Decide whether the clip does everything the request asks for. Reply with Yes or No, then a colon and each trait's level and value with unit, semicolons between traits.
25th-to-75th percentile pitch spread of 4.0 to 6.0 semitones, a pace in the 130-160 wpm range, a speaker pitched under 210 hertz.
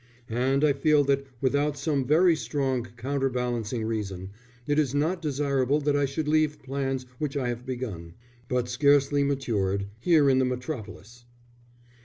No: average, 2.8 semitones; average, 150 wpm; low, 135 Hz